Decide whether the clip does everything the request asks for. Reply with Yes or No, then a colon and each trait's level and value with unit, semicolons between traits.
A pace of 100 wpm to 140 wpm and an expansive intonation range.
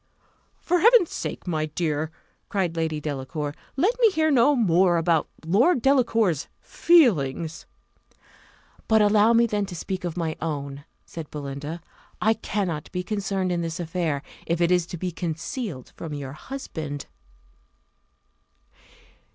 Yes: slow, 135 wpm; wide, 5.8 semitones